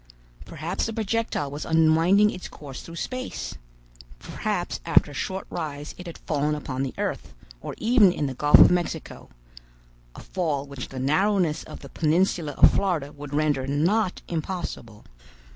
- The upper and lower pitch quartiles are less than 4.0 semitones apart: No, average, 4.6 semitones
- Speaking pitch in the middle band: Yes, medium, 155 Hz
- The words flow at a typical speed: Yes, average, 155 wpm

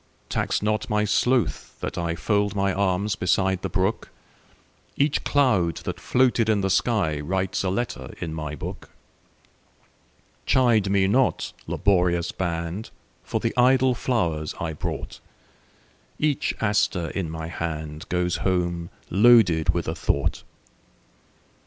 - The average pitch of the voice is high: No, very low, 95 Hz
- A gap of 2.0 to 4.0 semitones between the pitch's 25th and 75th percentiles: No, average, 4.4 semitones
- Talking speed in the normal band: No, slow, 110 wpm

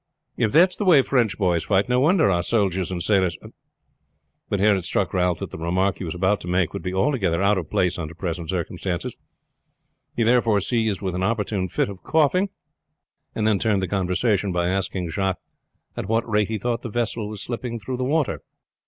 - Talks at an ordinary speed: No, fast, 210 wpm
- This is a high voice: No, low, 100 Hz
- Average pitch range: Yes, average, 4.1 semitones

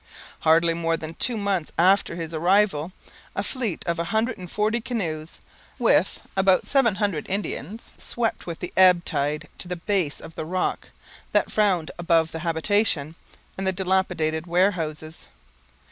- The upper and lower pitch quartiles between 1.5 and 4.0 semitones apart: Yes, average, 3.7 semitones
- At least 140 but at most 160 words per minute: Yes, average, 155 wpm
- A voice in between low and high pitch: Yes, medium, 180 Hz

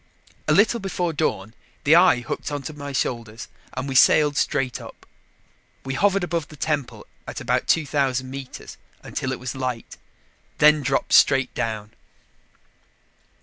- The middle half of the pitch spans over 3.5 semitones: No, average, 3.2 semitones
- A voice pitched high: No, medium, 140 Hz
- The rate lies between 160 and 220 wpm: No, average, 145 wpm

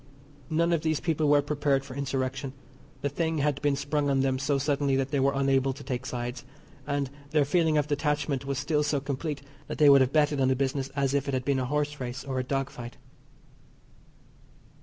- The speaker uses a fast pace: Yes, fast, 215 wpm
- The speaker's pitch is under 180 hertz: Yes, medium, 140 Hz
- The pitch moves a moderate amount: No, narrow, 1.8 semitones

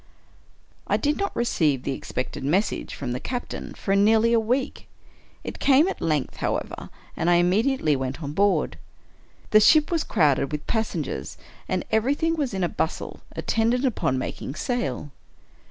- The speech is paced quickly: No, average, 165 wpm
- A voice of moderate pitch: No, high, 210 Hz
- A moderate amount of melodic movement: No, wide, 8.8 semitones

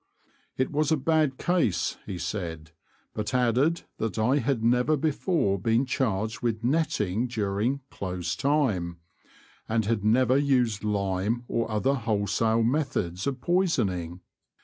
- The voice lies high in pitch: No, low, 115 Hz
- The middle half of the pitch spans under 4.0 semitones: No, average, 5.3 semitones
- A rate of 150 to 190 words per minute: No, average, 140 wpm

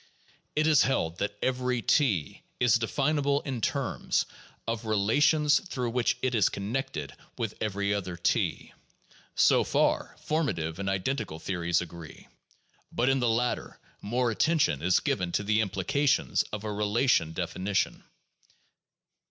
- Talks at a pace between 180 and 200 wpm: No, slow, 135 wpm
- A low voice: Yes, low, 110 Hz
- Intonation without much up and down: No, wide, 5.6 semitones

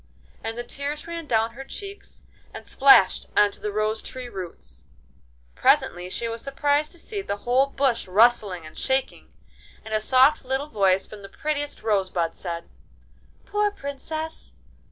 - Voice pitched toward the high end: Yes, high, 240 Hz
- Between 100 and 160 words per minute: Yes, average, 155 wpm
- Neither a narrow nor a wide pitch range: No, wide, 6.0 semitones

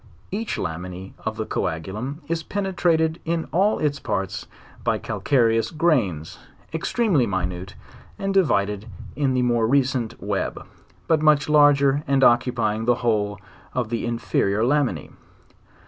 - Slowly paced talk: Yes, slow, 130 wpm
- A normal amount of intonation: No, wide, 6.4 semitones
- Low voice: Yes, low, 125 Hz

